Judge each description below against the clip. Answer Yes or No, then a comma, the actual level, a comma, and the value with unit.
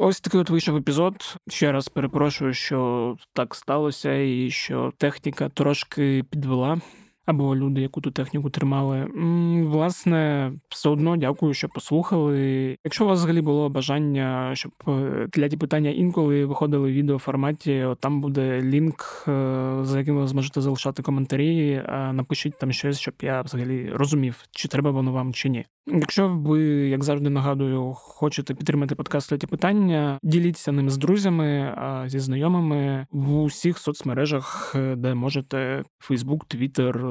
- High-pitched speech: No, medium, 140 Hz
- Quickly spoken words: No, average, 145 wpm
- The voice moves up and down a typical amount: No, narrow, 2.3 semitones